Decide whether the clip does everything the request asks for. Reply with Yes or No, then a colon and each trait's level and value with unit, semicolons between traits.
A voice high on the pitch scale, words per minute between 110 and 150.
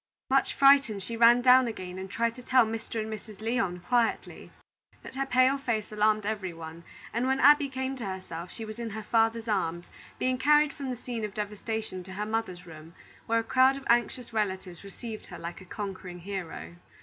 No: high, 220 Hz; average, 200 wpm